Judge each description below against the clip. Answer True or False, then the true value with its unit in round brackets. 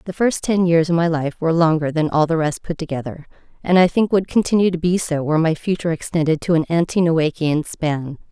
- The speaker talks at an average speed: False (230 wpm)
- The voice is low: False (165 Hz)